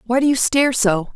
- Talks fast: Yes, fast, 260 wpm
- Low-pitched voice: No, high, 240 Hz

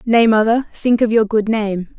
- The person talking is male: No, female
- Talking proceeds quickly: Yes, fast, 210 wpm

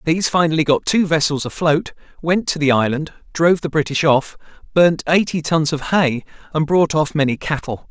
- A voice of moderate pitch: Yes, medium, 155 Hz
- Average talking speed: Yes, average, 180 wpm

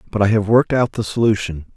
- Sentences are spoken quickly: Yes, fast, 240 wpm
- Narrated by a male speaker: Yes, male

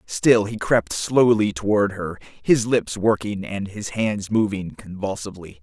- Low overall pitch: Yes, low, 100 Hz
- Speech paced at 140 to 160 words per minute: Yes, average, 150 wpm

